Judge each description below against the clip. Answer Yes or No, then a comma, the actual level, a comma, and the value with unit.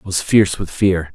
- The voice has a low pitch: Yes, very low, 90 Hz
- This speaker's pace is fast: Yes, fast, 260 wpm